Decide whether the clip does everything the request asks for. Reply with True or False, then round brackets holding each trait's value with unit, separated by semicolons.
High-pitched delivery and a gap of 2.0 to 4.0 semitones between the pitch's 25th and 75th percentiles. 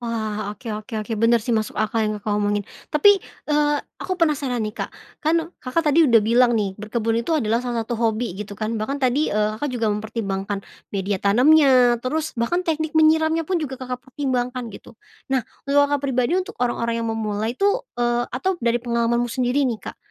False (240 Hz; 4.8 semitones)